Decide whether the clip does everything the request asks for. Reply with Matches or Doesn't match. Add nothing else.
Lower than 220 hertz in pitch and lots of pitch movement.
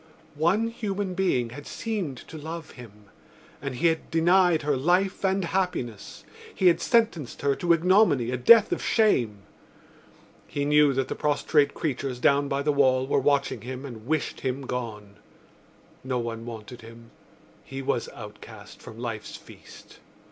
Matches